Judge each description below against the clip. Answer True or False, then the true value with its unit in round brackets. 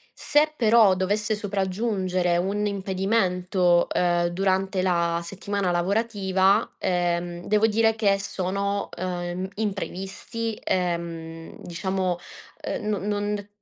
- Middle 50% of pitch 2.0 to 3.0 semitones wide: True (2.5 semitones)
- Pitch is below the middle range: False (190 Hz)